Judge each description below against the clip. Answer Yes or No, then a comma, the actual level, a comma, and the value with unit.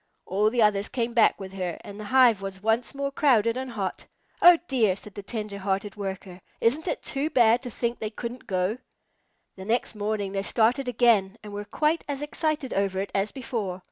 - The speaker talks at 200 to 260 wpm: Yes, fast, 205 wpm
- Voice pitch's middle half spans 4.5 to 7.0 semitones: No, average, 4.0 semitones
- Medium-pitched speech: No, high, 220 Hz